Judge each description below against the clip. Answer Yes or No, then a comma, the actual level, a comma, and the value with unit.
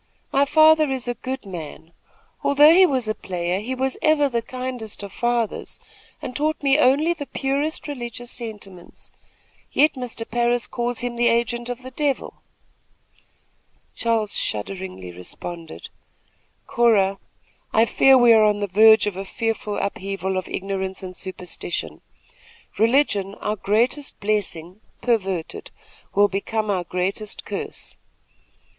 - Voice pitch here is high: Yes, high, 225 Hz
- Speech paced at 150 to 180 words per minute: No, slow, 135 wpm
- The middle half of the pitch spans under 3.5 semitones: No, average, 4.8 semitones